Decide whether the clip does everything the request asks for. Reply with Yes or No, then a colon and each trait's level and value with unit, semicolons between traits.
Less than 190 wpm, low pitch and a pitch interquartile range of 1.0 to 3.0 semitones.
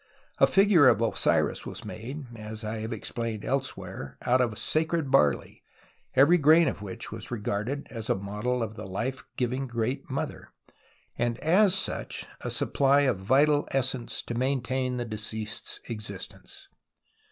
No: average, 160 wpm; low, 125 Hz; average, 4.3 semitones